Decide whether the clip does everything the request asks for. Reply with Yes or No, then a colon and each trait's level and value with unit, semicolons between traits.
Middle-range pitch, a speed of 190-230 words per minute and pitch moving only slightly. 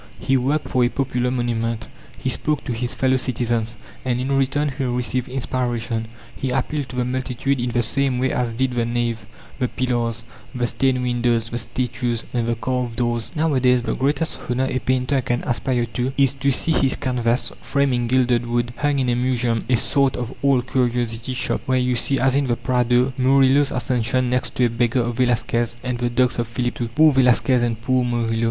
No: low, 125 Hz; average, 200 wpm; narrow, 1.6 semitones